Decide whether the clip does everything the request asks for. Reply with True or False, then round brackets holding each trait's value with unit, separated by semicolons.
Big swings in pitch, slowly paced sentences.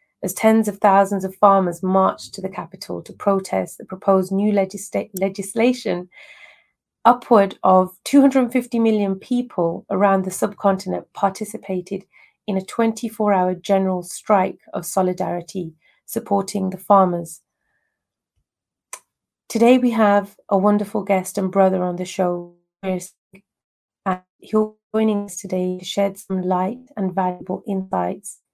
False (2.5 semitones; 125 wpm)